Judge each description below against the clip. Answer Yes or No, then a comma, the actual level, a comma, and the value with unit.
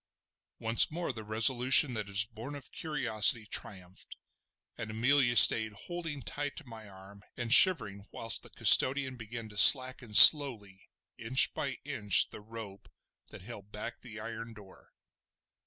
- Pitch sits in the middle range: No, low, 115 Hz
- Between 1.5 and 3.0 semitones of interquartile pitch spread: No, average, 3.8 semitones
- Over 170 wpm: No, average, 145 wpm